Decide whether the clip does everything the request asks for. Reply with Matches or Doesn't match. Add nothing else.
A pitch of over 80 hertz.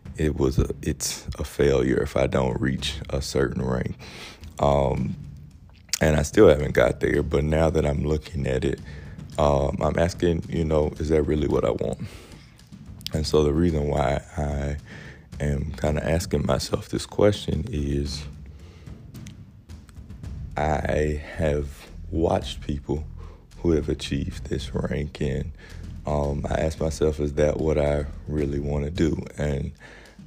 Doesn't match